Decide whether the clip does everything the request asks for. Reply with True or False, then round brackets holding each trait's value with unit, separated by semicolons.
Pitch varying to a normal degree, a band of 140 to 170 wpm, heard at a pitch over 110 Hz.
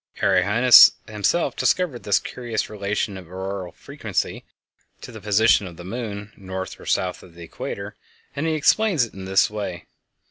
False (3.9 semitones; 165 wpm; 105 Hz)